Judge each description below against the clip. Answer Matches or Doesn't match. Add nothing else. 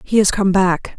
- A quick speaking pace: Matches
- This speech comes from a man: Doesn't match